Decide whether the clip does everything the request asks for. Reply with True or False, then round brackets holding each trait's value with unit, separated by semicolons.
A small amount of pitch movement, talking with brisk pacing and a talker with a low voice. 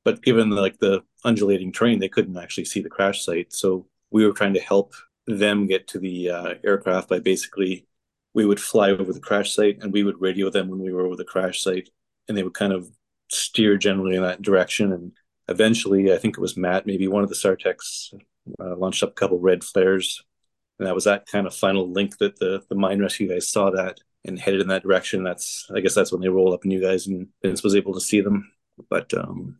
True (1.5 semitones; 235 wpm; 95 Hz)